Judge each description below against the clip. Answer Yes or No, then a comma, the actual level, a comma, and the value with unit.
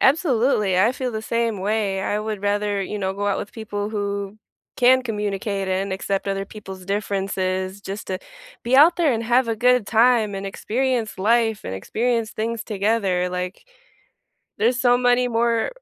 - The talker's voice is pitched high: Yes, high, 210 Hz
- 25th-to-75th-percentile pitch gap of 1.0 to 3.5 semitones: Yes, average, 3.2 semitones